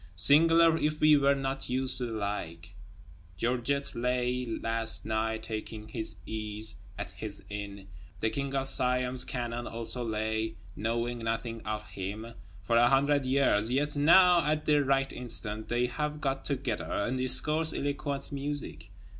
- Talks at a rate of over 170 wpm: No, average, 150 wpm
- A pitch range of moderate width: Yes, average, 4.0 semitones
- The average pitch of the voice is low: Yes, low, 125 Hz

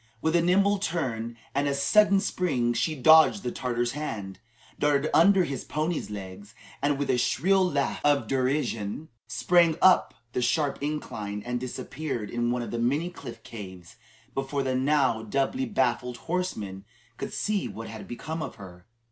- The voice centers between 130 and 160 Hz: Yes, low, 135 Hz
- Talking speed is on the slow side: No, average, 165 wpm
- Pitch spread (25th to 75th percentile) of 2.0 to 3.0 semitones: No, average, 5.2 semitones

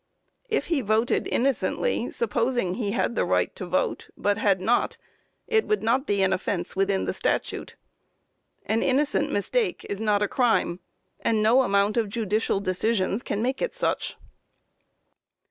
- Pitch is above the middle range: Yes, high, 220 Hz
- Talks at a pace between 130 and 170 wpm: Yes, average, 155 wpm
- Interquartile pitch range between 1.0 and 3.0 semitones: No, average, 4.3 semitones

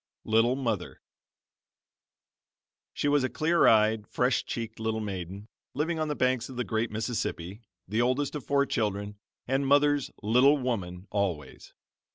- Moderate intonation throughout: Yes, average, 4.7 semitones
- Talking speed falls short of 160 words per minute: Yes, average, 145 wpm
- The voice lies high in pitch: No, low, 115 Hz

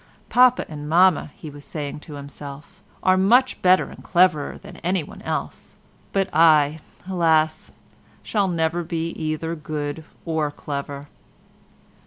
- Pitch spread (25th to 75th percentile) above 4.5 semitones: No, average, 3.7 semitones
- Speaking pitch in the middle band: Yes, medium, 160 Hz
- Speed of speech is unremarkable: No, slow, 130 wpm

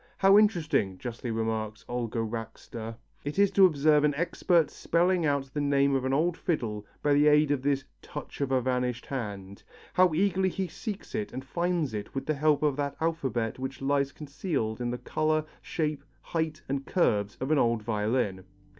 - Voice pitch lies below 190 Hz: Yes, medium, 140 Hz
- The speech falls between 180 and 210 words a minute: Yes, average, 185 wpm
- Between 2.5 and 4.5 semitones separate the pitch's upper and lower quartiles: No, average, 5.0 semitones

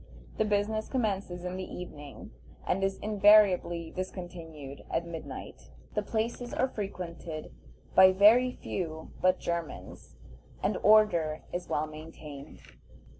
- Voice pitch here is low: No, medium, 185 Hz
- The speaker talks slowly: Yes, slow, 120 wpm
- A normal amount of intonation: Yes, average, 4.2 semitones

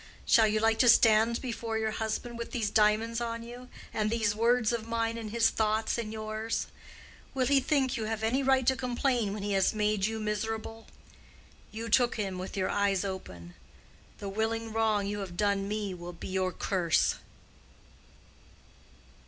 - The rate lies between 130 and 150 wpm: No, average, 175 wpm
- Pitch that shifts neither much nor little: No, narrow, 2.0 semitones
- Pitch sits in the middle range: No, high, 220 Hz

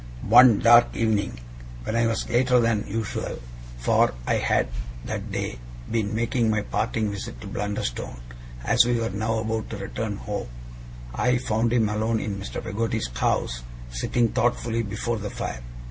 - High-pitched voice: No, low, 110 Hz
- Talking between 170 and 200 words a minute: No, average, 160 wpm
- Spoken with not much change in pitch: Yes, narrow, 2.1 semitones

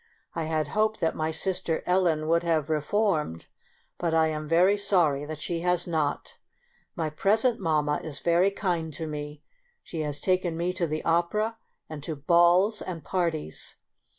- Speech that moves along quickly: No, average, 170 wpm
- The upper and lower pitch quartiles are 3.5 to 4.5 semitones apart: No, average, 2.8 semitones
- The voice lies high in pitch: No, medium, 165 Hz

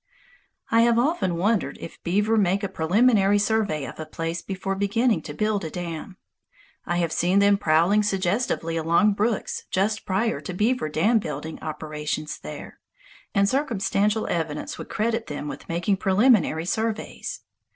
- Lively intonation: No, average, 4.7 semitones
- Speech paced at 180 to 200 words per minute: No, average, 150 wpm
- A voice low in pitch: No, high, 195 Hz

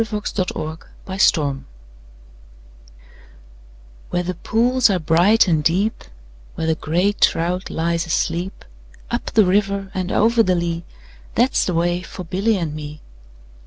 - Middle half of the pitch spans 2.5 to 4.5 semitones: Yes, average, 3.5 semitones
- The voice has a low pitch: No, medium, 180 Hz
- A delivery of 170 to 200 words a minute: No, slow, 135 wpm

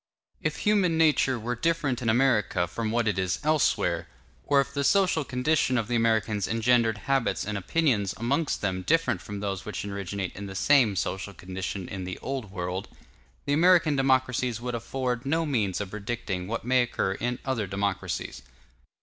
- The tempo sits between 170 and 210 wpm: Yes, average, 175 wpm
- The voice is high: No, low, 115 Hz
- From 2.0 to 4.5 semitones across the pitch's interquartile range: No, average, 5.3 semitones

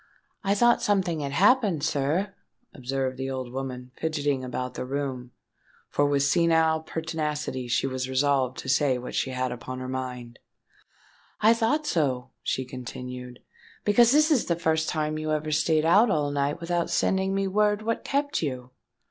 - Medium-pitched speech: Yes, medium, 145 Hz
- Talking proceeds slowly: No, average, 165 wpm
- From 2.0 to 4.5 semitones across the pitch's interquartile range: No, average, 5.3 semitones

